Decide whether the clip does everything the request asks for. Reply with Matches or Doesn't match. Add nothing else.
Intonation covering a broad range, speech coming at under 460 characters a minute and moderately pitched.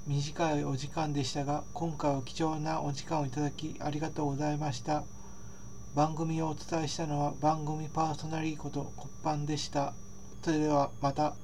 Doesn't match